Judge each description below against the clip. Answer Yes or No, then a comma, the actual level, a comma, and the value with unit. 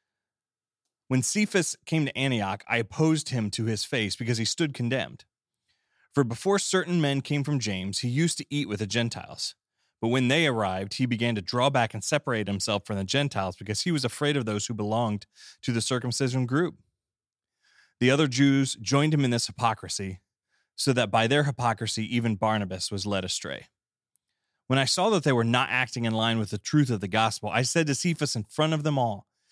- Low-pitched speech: Yes, low, 120 Hz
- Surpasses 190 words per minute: Yes, average, 200 wpm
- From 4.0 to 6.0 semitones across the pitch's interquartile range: Yes, average, 4.7 semitones